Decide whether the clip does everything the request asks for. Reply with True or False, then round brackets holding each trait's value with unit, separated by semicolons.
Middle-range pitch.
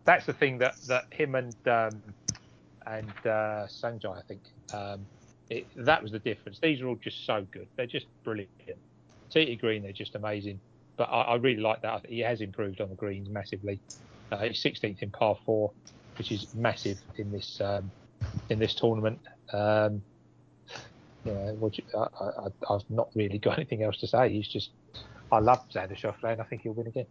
False (110 Hz)